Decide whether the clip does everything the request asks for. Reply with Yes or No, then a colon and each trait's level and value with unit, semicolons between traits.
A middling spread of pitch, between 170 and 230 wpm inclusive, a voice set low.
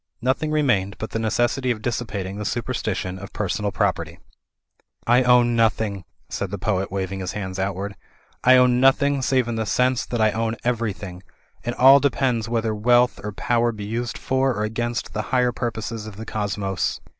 Yes: average, 3.3 semitones; average, 180 wpm; low, 115 Hz